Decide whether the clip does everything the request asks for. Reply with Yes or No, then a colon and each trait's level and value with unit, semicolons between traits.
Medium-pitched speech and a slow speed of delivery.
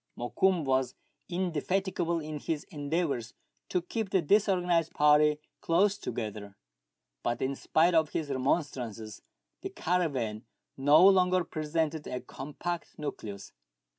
Yes: medium, 155 Hz; slow, 115 wpm